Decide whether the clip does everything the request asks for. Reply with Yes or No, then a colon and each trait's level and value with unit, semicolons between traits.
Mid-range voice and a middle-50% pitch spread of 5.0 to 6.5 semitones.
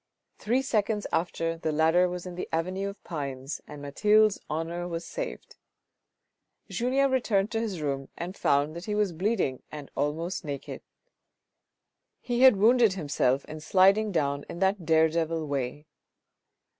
Yes: medium, 175 Hz; wide, 5.4 semitones